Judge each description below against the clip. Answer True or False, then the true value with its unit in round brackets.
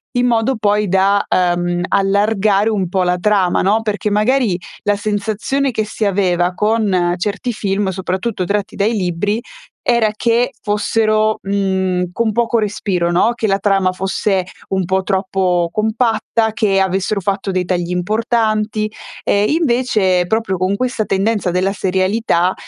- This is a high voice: True (200 Hz)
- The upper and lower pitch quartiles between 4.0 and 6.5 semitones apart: False (2.6 semitones)